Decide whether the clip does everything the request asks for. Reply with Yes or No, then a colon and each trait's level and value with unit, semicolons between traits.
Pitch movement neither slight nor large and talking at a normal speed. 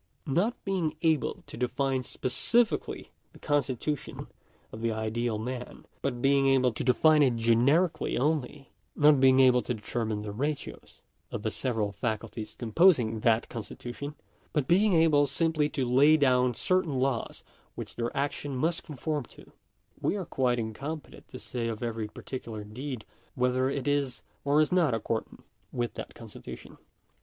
Yes: average, 4.1 semitones; average, 155 wpm